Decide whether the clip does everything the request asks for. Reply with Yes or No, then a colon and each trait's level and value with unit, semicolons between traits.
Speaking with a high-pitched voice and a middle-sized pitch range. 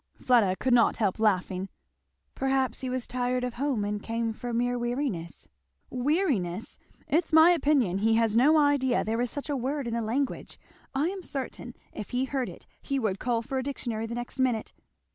Yes: high, 245 Hz; average, 3.3 semitones